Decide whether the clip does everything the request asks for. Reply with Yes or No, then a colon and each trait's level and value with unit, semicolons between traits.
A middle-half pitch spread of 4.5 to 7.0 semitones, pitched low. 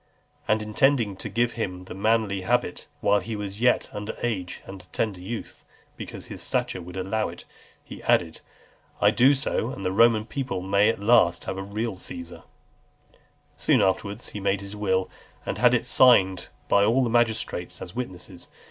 No: average, 3.4 semitones; low, 105 Hz